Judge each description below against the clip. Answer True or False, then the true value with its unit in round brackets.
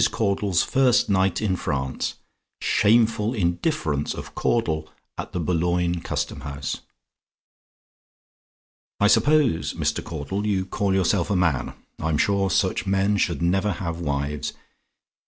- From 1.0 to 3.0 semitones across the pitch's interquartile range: False (4.1 semitones)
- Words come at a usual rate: False (120 wpm)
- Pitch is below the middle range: True (95 Hz)